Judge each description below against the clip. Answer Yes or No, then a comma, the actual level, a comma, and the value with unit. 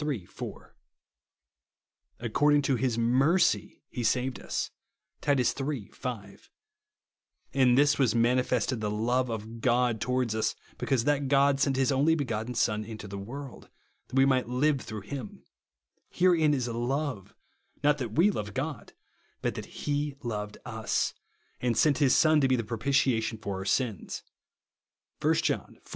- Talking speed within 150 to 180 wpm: Yes, average, 155 wpm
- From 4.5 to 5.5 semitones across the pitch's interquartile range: No, average, 3.9 semitones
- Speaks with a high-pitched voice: No, low, 125 Hz